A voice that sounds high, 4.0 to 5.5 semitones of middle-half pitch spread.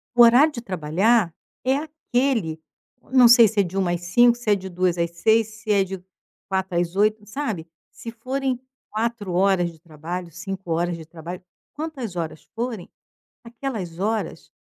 Yes: high, 200 Hz; average, 5.2 semitones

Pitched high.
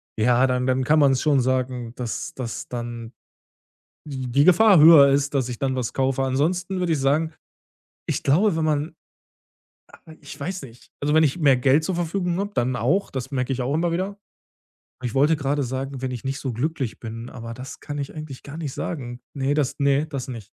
No: low, 135 Hz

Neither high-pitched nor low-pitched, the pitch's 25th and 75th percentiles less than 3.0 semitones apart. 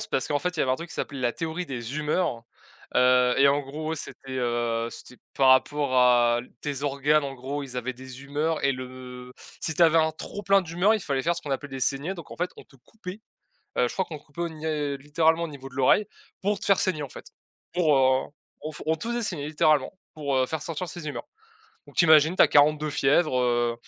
No: medium, 145 Hz; average, 3.7 semitones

